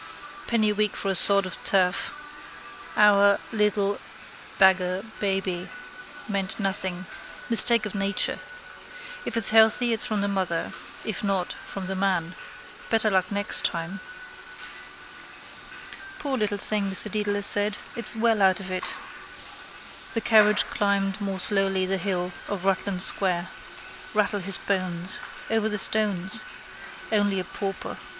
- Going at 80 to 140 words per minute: Yes, slow, 135 wpm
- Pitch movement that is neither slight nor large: No, narrow, 1.9 semitones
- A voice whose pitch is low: No, high, 200 Hz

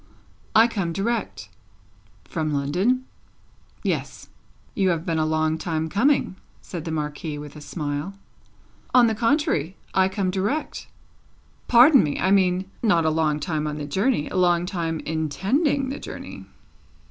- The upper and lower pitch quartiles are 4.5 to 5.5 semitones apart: Yes, average, 5.2 semitones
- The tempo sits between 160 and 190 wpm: No, average, 145 wpm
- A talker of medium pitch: Yes, medium, 175 Hz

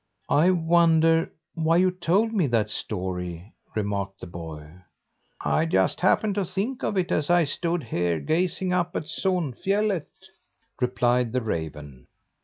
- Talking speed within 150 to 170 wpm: No, average, 140 wpm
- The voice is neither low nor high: Yes, medium, 160 Hz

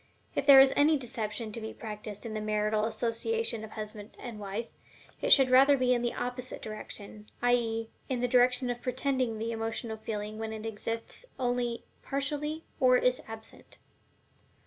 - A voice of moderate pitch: No, high, 235 Hz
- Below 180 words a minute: Yes, average, 170 wpm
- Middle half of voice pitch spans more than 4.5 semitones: No, average, 2.7 semitones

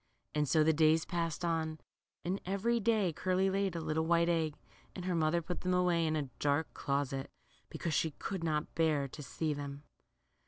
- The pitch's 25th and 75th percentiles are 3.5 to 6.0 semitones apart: No, average, 2.8 semitones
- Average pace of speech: Yes, average, 190 wpm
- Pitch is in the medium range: Yes, medium, 160 Hz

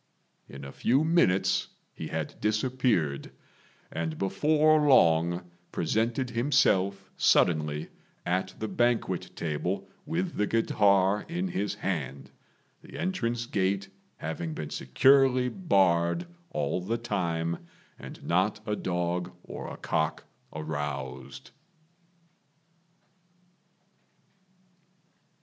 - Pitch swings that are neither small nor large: No, wide, 6.2 semitones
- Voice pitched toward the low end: Yes, very low, 95 Hz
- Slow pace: Yes, slow, 95 wpm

